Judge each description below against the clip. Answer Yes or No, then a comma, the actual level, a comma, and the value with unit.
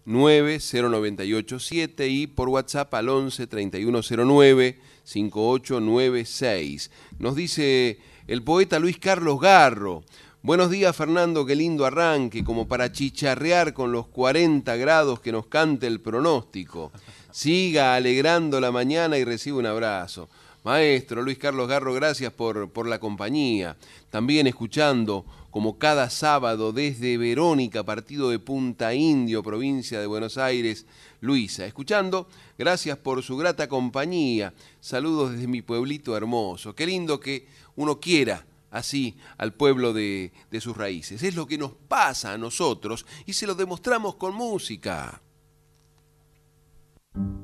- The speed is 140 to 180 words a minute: No, average, 130 wpm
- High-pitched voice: No, low, 130 Hz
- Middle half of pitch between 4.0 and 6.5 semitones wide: Yes, average, 4.8 semitones